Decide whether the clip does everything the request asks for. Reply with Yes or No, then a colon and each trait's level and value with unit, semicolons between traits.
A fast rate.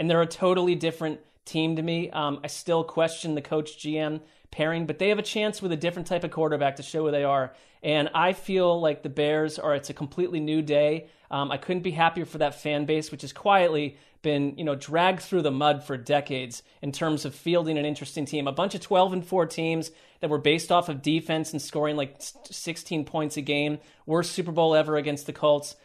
Yes: fast, 230 wpm